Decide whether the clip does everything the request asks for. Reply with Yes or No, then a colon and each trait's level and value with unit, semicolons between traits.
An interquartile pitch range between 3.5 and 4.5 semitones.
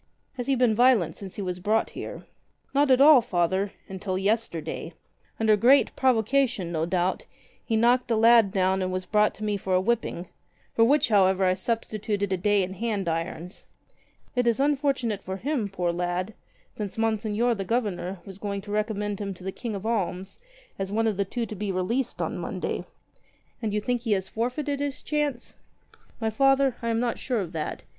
Yes: average, 4.0 semitones